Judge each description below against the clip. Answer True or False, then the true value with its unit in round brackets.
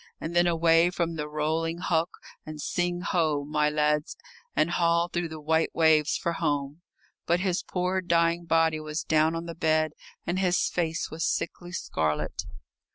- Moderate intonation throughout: False (2.0 semitones)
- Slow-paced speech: False (165 wpm)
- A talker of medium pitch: True (165 Hz)